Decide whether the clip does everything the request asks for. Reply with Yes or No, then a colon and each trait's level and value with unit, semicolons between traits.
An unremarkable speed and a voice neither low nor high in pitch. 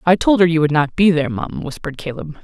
No: fast, 270 wpm; medium, 165 Hz